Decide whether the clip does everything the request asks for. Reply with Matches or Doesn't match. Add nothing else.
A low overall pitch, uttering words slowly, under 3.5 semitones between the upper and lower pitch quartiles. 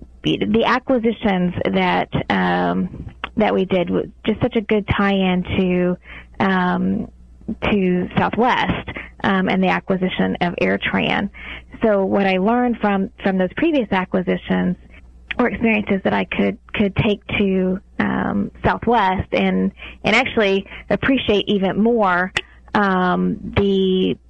Doesn't match